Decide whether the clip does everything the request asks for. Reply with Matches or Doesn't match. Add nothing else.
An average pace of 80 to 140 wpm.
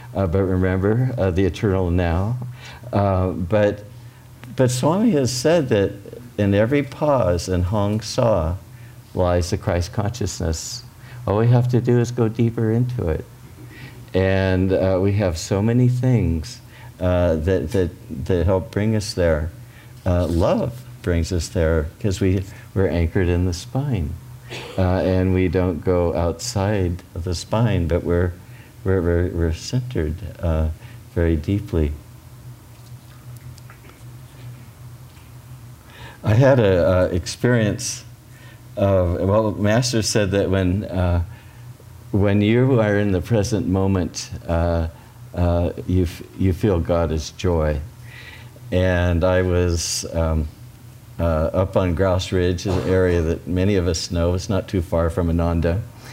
Matches